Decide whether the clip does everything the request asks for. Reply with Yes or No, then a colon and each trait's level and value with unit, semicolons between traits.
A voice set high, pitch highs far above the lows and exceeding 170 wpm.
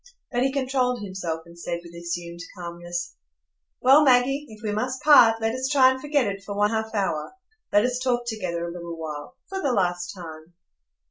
Yes: high, 210 Hz; wide, 6.8 semitones; average, 195 wpm